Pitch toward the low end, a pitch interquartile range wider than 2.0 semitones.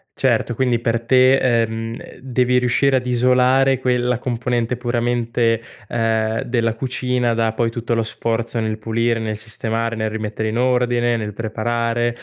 No: low, 120 Hz; narrow, 1.6 semitones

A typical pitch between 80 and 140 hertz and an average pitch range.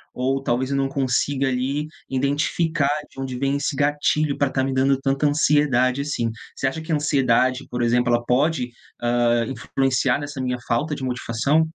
No: low, 135 Hz; narrow, 2.3 semitones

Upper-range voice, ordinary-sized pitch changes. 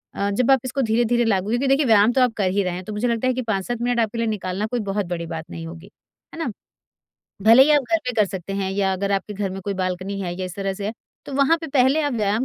Yes: high, 210 Hz; average, 4.3 semitones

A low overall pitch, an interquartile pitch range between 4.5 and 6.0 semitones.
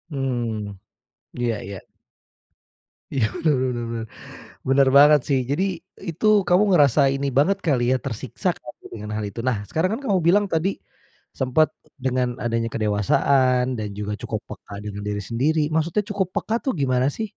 Yes: low, 130 Hz; wide, 5.5 semitones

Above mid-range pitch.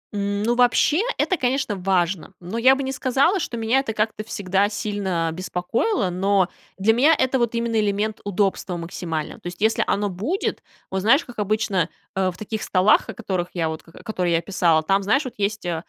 Yes: high, 205 Hz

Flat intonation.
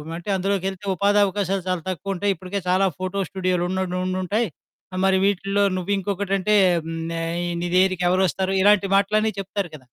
Yes: narrow, 1.6 semitones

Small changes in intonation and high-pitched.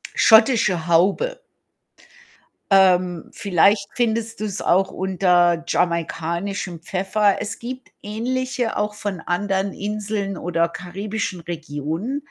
No: average, 3.5 semitones; high, 195 Hz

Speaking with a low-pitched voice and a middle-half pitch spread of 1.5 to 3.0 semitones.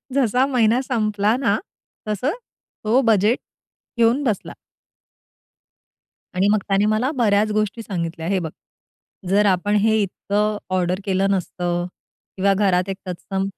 No: high, 205 Hz; narrow, 2.4 semitones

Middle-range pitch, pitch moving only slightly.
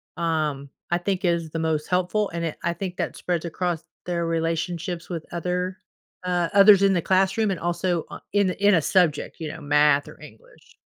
Yes: medium, 175 Hz; narrow, 2.3 semitones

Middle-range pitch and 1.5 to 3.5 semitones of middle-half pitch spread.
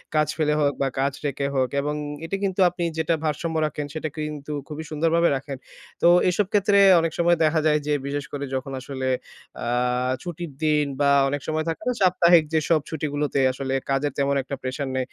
Yes: medium, 150 Hz; average, 2.8 semitones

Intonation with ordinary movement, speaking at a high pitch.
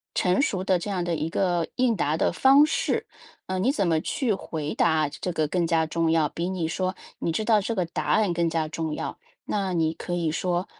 No: average, 3.0 semitones; medium, 175 Hz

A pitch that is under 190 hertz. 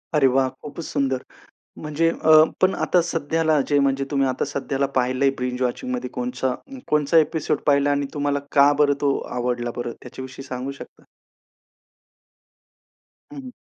Yes: medium, 140 Hz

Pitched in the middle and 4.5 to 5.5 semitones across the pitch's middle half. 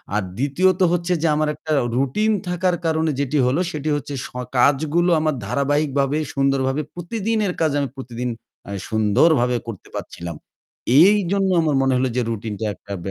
Yes: medium, 145 Hz; average, 5.0 semitones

